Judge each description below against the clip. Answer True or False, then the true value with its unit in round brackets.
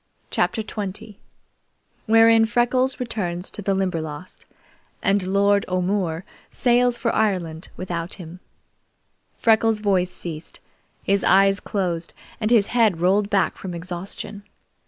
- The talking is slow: True (115 wpm)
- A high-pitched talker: True (195 Hz)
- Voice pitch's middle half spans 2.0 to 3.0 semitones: False (3.5 semitones)